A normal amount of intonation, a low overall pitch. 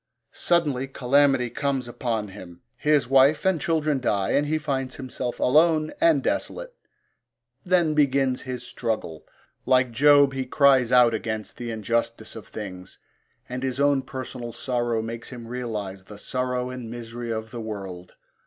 Yes: average, 3.6 semitones; low, 125 Hz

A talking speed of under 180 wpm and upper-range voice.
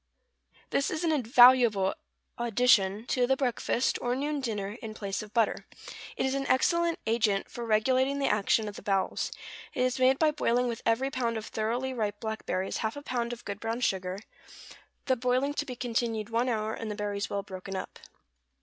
No: average, 195 wpm; high, 235 Hz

